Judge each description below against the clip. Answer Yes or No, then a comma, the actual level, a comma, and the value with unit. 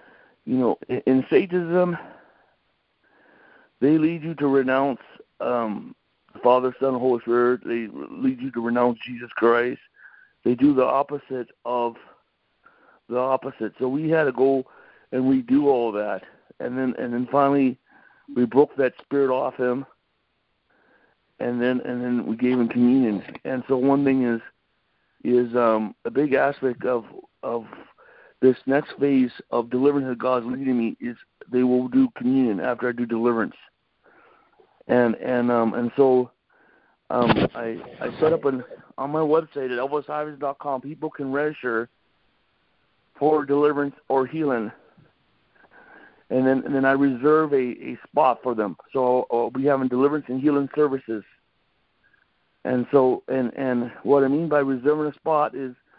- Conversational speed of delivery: Yes, average, 150 wpm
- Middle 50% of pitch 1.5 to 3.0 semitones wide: Yes, average, 2.7 semitones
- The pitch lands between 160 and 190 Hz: No, low, 130 Hz